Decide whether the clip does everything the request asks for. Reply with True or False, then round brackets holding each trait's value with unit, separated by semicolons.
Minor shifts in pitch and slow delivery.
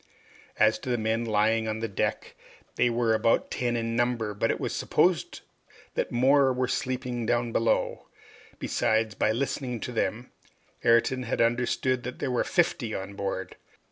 False (2.1 semitones; 175 wpm)